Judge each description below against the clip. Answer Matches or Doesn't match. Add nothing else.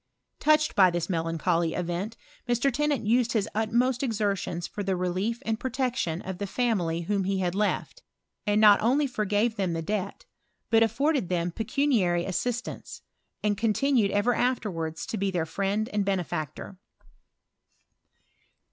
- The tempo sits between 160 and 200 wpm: Doesn't match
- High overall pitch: Matches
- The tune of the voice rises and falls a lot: Doesn't match